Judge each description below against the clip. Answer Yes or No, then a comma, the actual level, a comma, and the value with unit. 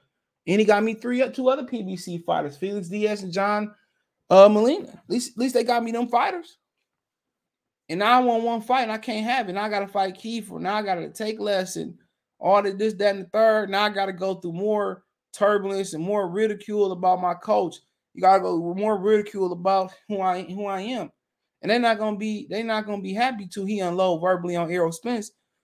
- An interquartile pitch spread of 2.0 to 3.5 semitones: Yes, average, 2.7 semitones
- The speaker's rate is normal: No, fast, 225 wpm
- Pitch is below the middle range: No, high, 205 Hz